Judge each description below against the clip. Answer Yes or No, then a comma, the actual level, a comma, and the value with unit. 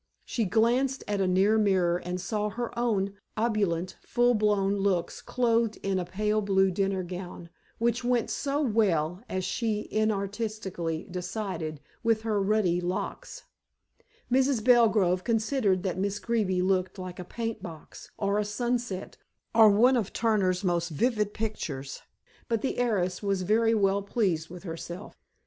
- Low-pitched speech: No, high, 200 Hz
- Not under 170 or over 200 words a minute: No, average, 150 wpm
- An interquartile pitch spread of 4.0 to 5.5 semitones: No, average, 3.6 semitones